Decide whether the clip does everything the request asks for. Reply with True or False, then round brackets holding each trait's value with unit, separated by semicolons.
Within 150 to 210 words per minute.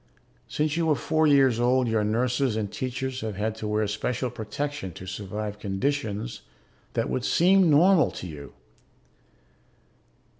False (140 wpm)